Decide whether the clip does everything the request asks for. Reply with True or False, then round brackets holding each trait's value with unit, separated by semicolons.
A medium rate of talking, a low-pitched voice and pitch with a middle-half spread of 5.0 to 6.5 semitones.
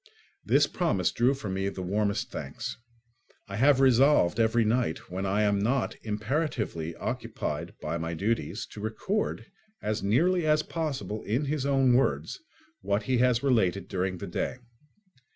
True (150 wpm; 110 Hz; 5.5 semitones)